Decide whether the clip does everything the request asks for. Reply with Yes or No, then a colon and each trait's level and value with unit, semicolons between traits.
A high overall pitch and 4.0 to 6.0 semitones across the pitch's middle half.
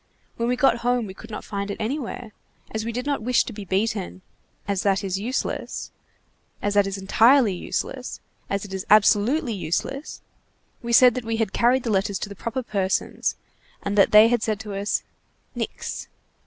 No: high, 215 Hz; average, 3.3 semitones